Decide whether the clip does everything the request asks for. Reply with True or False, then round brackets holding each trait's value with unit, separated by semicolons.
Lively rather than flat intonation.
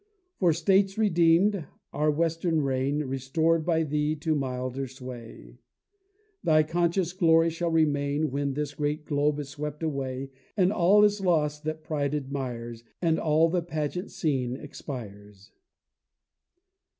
False (3.3 semitones)